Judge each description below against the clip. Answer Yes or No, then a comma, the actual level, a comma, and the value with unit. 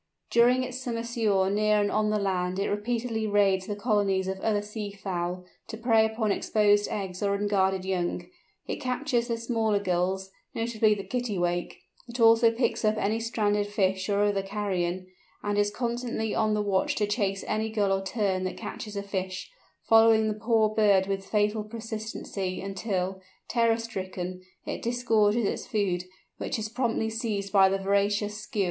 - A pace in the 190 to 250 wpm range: No, average, 170 wpm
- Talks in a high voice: Yes, high, 210 Hz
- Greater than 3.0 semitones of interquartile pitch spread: No, narrow, 2.6 semitones